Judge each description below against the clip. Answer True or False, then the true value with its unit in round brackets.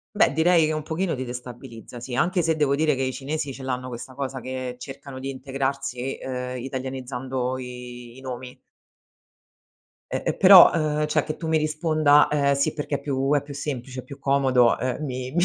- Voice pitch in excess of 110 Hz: True (135 Hz)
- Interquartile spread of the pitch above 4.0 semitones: False (2.9 semitones)